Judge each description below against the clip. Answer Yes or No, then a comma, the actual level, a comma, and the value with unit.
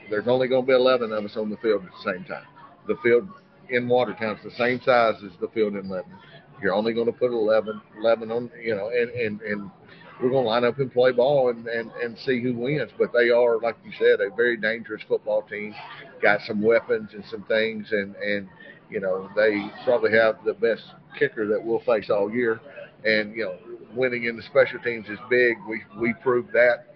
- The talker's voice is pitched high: No, low, 120 Hz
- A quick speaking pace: Yes, fast, 225 wpm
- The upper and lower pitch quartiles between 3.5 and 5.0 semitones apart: No, average, 3.1 semitones